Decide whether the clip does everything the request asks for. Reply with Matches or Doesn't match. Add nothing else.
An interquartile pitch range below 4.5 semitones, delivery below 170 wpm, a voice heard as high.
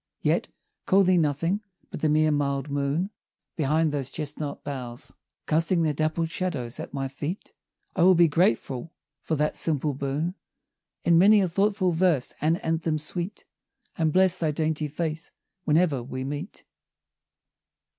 Doesn't match